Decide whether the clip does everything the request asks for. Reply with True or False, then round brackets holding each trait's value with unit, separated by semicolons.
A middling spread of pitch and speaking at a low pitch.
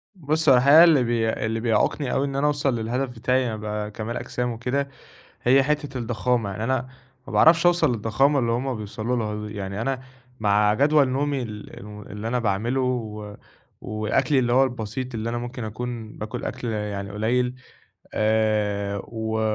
True (3.5 semitones; 120 Hz)